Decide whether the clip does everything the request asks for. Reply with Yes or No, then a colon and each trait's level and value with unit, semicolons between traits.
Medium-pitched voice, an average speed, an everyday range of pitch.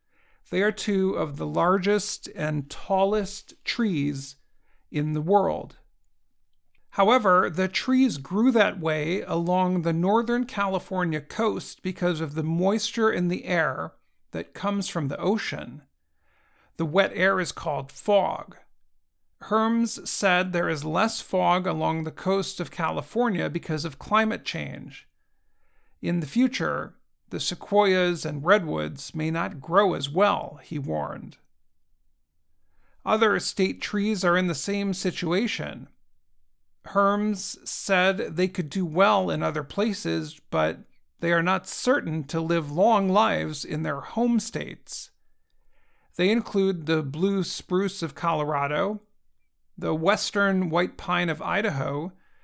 No: medium, 180 Hz; slow, 130 wpm; average, 4.7 semitones